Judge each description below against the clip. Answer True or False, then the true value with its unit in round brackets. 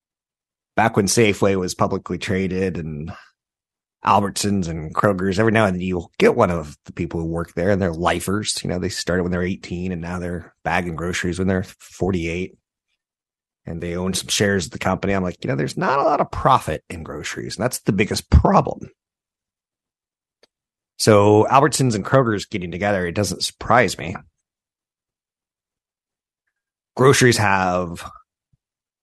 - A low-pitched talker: True (95 Hz)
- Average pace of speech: True (160 wpm)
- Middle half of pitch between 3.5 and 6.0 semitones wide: False (2.7 semitones)